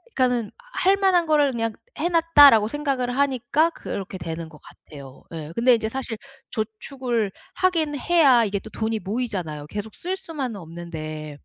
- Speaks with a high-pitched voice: Yes, high, 235 Hz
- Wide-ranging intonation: Yes, wide, 7.1 semitones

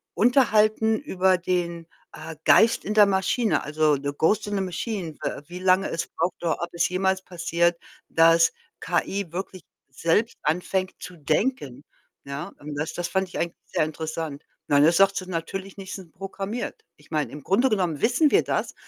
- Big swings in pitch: No, average, 3.3 semitones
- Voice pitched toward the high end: No, medium, 180 Hz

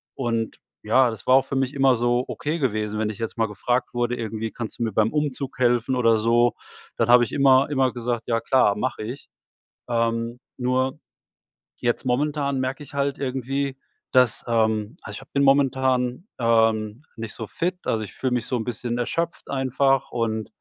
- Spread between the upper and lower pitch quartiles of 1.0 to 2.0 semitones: No, average, 2.7 semitones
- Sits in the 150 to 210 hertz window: No, low, 125 Hz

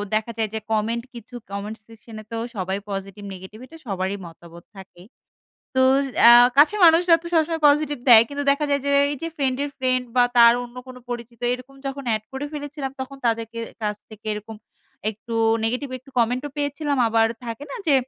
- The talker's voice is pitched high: Yes, high, 240 Hz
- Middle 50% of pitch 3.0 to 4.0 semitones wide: No, average, 4.6 semitones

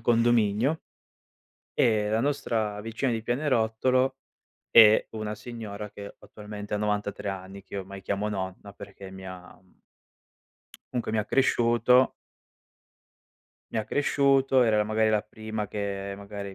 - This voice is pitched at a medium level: No, low, 105 Hz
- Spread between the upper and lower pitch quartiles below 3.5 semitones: Yes, narrow, 2.6 semitones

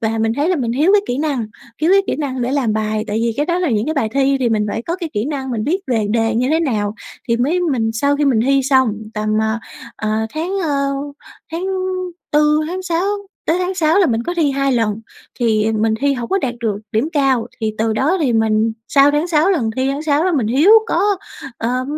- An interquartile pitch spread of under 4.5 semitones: No, wide, 5.5 semitones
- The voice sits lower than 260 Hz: No, very high, 265 Hz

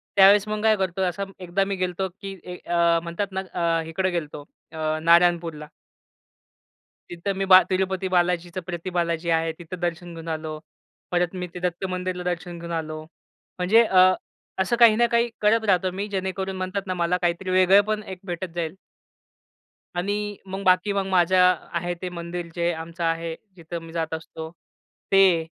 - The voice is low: No, medium, 180 Hz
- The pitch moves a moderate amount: No, narrow, 2.1 semitones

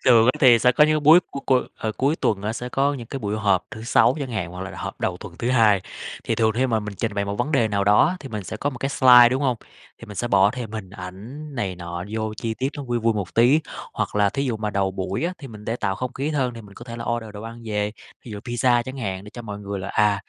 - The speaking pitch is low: Yes, low, 115 Hz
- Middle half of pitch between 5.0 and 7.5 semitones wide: No, average, 3.7 semitones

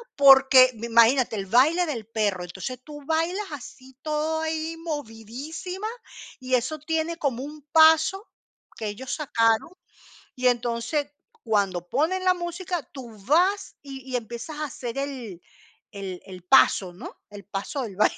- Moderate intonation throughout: No, wide, 5.9 semitones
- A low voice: No, very high, 265 Hz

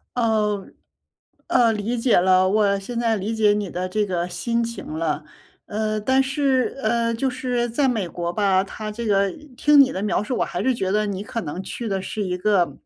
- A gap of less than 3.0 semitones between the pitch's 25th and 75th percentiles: No, average, 3.7 semitones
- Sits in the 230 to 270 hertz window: No, high, 210 Hz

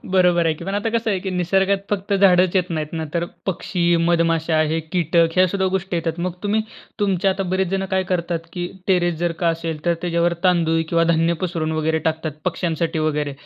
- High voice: No, medium, 175 Hz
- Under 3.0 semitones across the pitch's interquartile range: Yes, narrow, 2.4 semitones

